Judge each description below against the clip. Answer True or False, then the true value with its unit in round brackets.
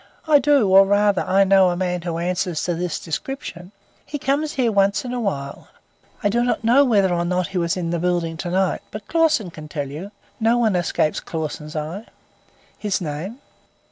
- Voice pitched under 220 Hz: True (190 Hz)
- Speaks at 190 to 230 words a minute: True (200 wpm)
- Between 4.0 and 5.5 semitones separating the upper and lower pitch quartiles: True (4.5 semitones)